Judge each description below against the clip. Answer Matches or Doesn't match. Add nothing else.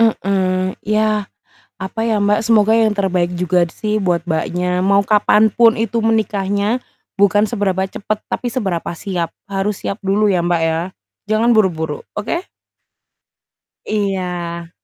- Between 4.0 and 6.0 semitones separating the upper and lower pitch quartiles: Doesn't match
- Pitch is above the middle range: Matches